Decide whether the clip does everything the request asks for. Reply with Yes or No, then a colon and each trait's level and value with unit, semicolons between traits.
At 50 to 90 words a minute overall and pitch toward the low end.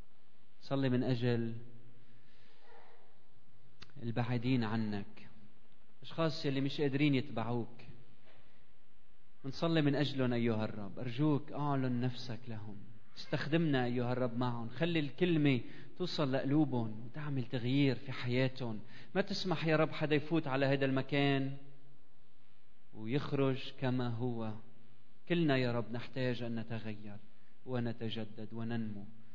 No: average, 105 wpm; low, 125 Hz